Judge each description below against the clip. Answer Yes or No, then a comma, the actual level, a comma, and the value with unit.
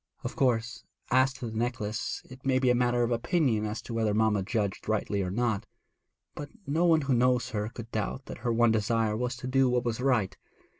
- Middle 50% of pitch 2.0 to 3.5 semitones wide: Yes, narrow, 2.6 semitones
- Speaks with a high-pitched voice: No, low, 120 Hz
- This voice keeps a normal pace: No, fast, 215 wpm